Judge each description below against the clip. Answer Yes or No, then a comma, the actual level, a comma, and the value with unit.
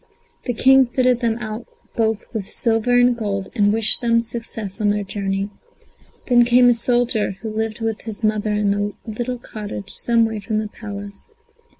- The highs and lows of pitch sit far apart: No, narrow, 2.5 semitones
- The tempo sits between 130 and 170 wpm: No, average, 180 wpm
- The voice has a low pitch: No, high, 220 Hz